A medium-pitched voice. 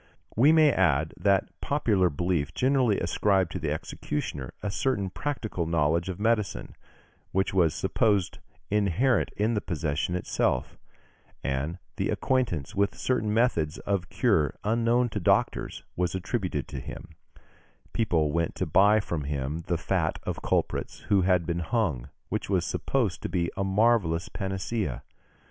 No: very low, 95 Hz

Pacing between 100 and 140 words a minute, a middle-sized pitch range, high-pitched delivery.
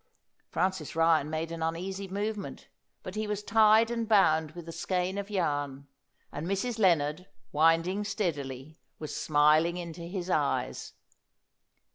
No: slow, 135 wpm; average, 4.1 semitones; medium, 175 Hz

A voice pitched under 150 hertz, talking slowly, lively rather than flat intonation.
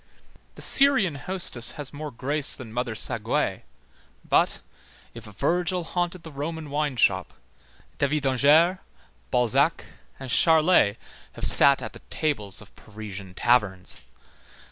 Yes: medium, 140 Hz; slow, 120 wpm; wide, 5.8 semitones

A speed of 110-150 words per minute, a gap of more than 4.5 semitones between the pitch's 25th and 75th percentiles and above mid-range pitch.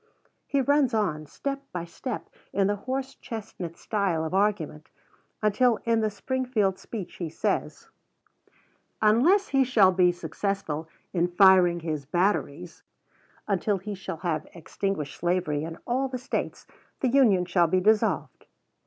Yes: average, 140 wpm; average, 5.2 semitones; high, 195 Hz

